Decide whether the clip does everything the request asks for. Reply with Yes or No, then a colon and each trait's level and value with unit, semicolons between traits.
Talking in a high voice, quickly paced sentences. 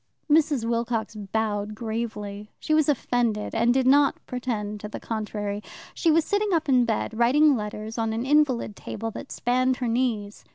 No: high, 235 Hz; average, 170 wpm